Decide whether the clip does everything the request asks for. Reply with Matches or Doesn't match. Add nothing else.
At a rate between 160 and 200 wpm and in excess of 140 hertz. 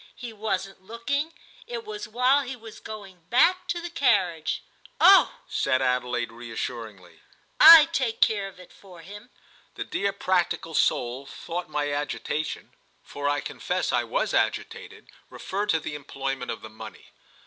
Doesn't match